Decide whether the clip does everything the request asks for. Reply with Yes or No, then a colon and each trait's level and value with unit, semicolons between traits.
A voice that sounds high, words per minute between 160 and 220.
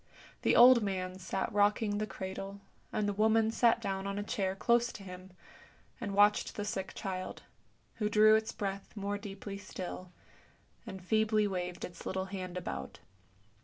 Yes: high, 200 Hz; average, 165 wpm